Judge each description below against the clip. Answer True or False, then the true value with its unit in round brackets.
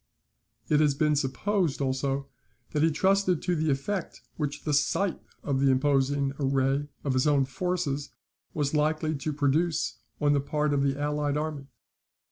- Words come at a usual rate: True (160 wpm)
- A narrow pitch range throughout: True (2.1 semitones)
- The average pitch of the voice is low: False (145 Hz)